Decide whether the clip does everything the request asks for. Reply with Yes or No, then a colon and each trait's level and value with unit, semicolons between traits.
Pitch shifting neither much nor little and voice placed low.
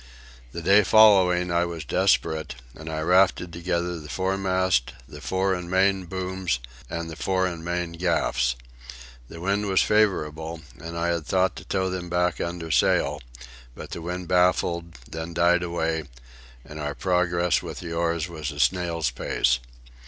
No: narrow, 2.2 semitones; very low, 85 Hz